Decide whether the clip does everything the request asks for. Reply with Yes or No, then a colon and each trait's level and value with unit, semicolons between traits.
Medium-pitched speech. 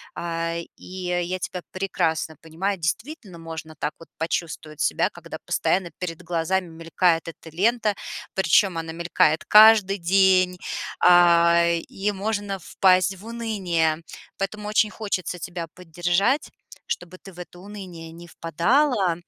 Yes: medium, 180 Hz